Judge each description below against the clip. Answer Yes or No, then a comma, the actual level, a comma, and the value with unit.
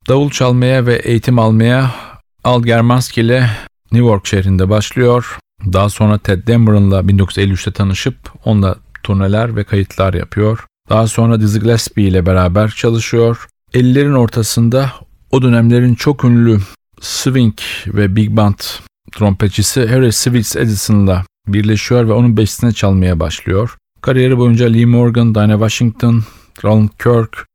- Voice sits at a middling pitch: No, low, 110 Hz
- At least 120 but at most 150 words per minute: Yes, average, 130 wpm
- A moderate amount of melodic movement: Yes, average, 3.1 semitones